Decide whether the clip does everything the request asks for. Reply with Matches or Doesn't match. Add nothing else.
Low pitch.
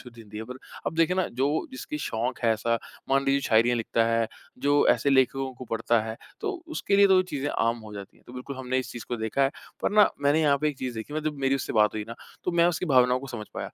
Matches